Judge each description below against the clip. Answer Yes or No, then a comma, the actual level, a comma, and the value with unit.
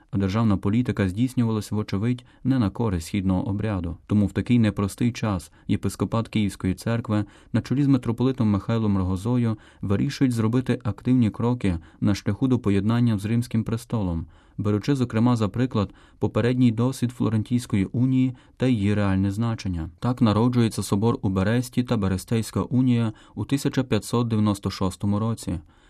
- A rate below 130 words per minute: No, average, 135 wpm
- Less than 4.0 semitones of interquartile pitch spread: Yes, average, 3.4 semitones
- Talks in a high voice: No, low, 110 Hz